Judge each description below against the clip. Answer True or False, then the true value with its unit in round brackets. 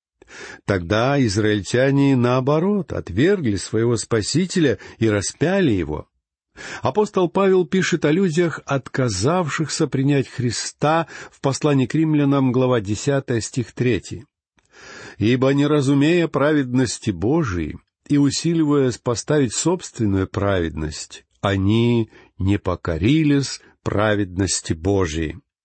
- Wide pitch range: True (6.1 semitones)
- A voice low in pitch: True (130 Hz)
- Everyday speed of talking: False (95 wpm)